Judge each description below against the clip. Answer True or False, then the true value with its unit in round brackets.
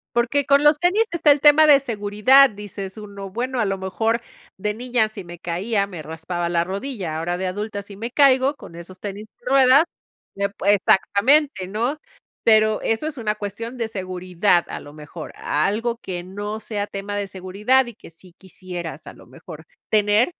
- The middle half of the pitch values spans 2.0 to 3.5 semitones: False (4.5 semitones)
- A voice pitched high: True (205 Hz)